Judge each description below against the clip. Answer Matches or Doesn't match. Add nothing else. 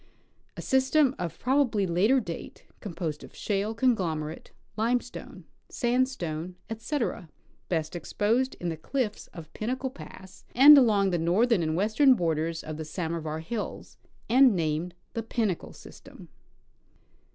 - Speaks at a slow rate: Matches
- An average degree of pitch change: Doesn't match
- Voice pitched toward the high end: Matches